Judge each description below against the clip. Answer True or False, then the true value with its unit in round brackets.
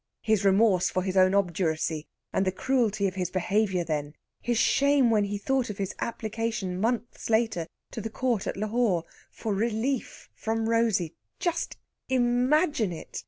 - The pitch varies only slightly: False (3.9 semitones)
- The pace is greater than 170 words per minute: False (160 wpm)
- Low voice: False (215 Hz)